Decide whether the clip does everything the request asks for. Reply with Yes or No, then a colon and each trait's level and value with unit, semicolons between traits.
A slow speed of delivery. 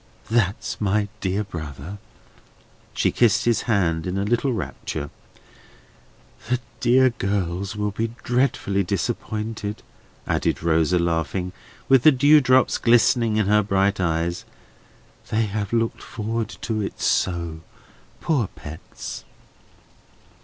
Yes: slow, 115 wpm